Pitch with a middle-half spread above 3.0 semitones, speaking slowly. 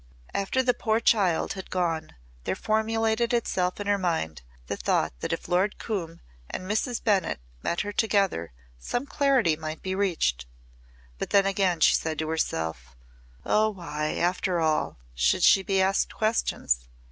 No: average, 5.3 semitones; average, 160 wpm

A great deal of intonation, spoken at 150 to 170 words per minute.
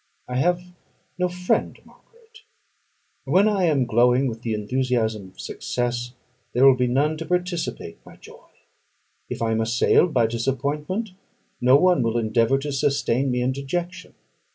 Yes: wide, 6.4 semitones; average, 155 wpm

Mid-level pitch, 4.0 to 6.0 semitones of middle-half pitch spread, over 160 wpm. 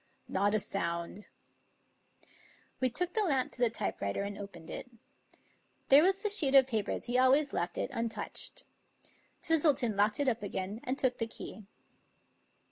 No: high, 235 Hz; average, 5.2 semitones; average, 170 wpm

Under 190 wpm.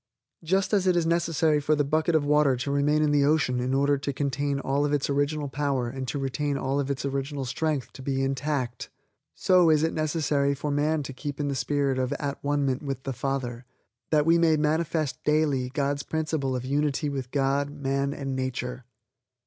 No: fast, 205 wpm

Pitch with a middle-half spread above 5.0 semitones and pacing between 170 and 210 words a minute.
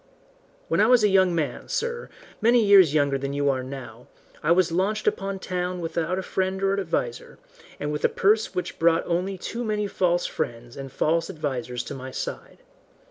Yes: wide, 5.6 semitones; average, 190 wpm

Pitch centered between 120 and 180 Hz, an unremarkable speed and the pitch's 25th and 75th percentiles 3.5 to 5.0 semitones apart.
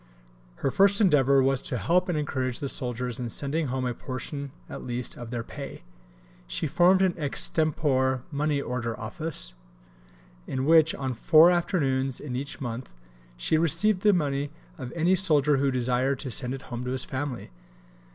Yes: medium, 140 Hz; average, 170 wpm; average, 3.9 semitones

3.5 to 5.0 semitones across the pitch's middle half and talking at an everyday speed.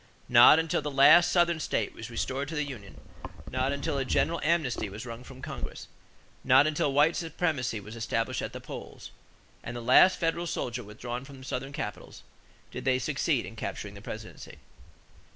Yes: average, 4.2 semitones; average, 175 wpm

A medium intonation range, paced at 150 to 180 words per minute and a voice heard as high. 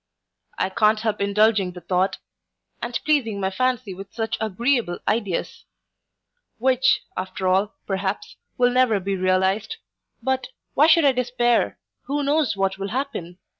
No: average, 4.8 semitones; average, 140 wpm; high, 215 Hz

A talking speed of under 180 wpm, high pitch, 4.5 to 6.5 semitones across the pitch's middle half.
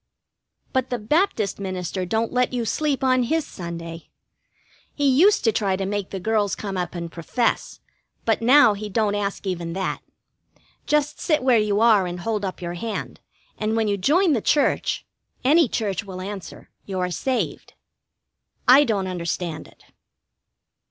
Yes: average, 165 wpm; high, 210 Hz; average, 5.2 semitones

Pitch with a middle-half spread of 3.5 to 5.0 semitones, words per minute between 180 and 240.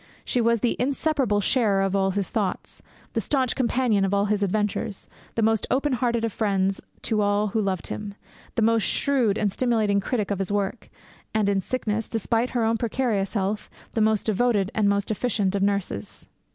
No: average, 2.7 semitones; average, 190 wpm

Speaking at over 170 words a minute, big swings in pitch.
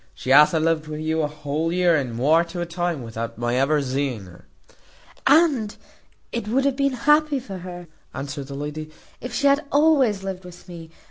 Yes: average, 200 wpm; wide, 8.1 semitones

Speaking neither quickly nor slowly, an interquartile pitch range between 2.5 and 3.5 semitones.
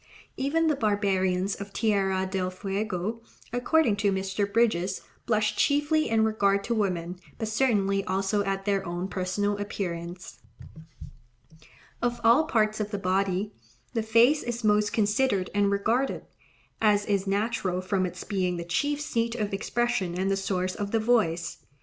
Yes: average, 150 wpm; average, 3.0 semitones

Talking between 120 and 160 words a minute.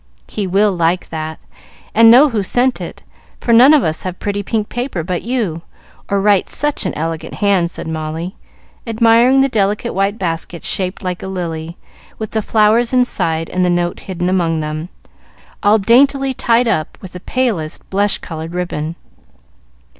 No: average, 170 wpm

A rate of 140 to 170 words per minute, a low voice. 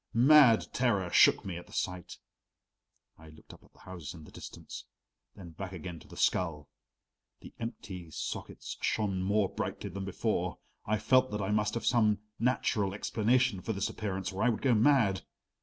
No: average, 180 wpm; low, 100 Hz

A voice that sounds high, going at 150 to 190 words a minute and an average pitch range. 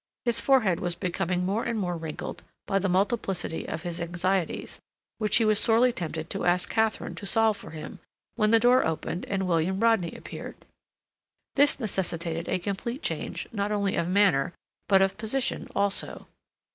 Yes: high, 195 Hz; average, 170 wpm; average, 4.1 semitones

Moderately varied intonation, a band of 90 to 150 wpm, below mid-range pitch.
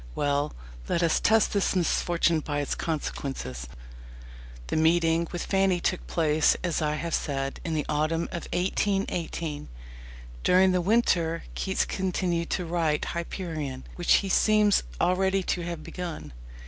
No: average, 3.0 semitones; average, 140 wpm; medium, 170 Hz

